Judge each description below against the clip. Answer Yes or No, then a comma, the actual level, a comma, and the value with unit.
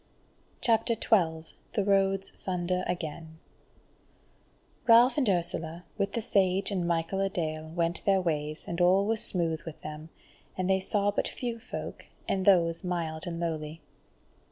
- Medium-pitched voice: Yes, medium, 180 Hz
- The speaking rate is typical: Yes, average, 150 wpm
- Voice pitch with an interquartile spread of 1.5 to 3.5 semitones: Yes, average, 3.2 semitones